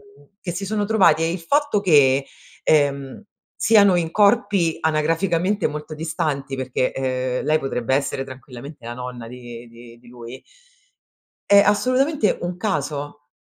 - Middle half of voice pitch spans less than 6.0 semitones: No, wide, 6.6 semitones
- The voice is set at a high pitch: No, medium, 150 Hz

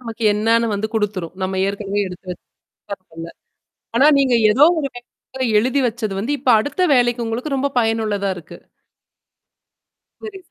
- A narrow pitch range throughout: No, average, 4.3 semitones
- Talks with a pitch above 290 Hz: No, high, 225 Hz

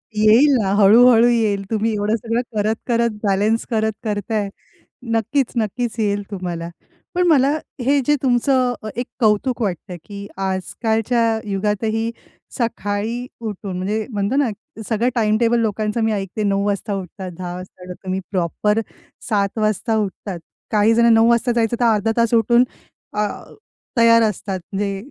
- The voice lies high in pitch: Yes, high, 215 Hz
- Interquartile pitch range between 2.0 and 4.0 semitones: Yes, narrow, 2.6 semitones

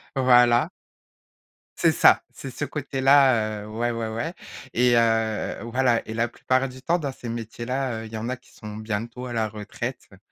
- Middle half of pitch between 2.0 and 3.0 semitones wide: Yes, narrow, 2.6 semitones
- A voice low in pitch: Yes, low, 120 Hz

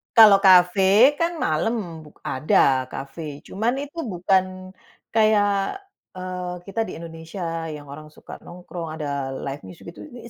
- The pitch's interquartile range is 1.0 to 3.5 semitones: No, average, 4.9 semitones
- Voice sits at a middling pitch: Yes, medium, 180 Hz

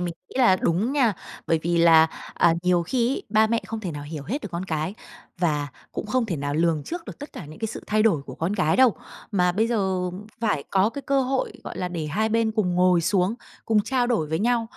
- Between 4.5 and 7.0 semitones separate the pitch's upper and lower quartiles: Yes, average, 5.2 semitones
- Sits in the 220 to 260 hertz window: No, high, 190 Hz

